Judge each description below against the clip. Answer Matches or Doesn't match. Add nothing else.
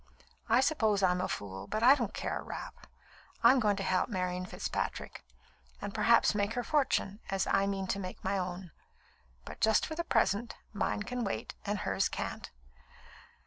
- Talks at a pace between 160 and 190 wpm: Matches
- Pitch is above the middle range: Matches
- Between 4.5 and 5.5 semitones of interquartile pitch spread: Doesn't match